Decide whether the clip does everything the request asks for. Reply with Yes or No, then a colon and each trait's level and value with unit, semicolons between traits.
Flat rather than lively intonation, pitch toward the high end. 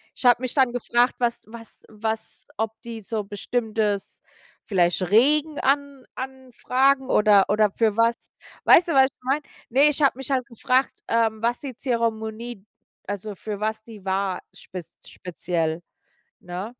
No: average, 3.7 semitones; high, 230 Hz